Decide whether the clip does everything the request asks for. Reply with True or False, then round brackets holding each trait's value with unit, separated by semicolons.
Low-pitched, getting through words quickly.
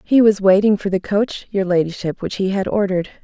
False (195 Hz; 220 wpm)